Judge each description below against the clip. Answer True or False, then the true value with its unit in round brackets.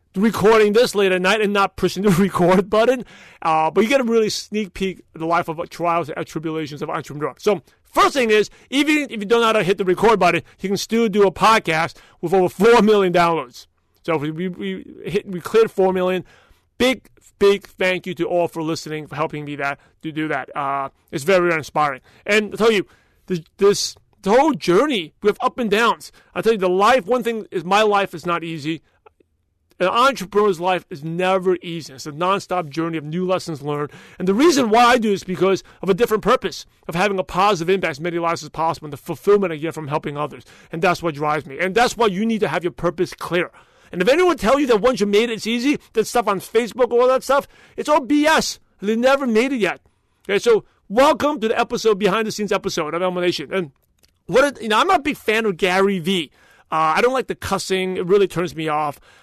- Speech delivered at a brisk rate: True (235 wpm)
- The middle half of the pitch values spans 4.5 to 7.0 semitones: True (4.9 semitones)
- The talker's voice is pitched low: False (190 Hz)